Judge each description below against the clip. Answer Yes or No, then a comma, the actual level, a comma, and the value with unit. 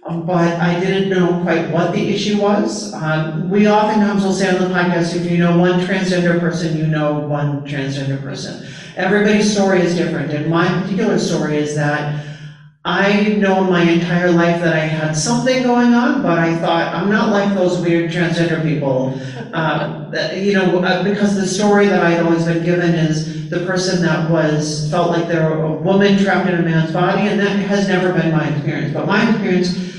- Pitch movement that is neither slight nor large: Yes, average, 3.4 semitones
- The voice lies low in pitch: No, medium, 175 Hz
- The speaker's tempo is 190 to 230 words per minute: Yes, average, 195 wpm